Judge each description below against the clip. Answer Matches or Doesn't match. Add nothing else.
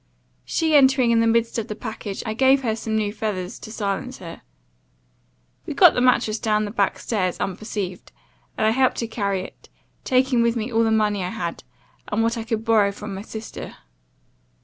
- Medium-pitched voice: Doesn't match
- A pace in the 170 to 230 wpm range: Matches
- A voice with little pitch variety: Matches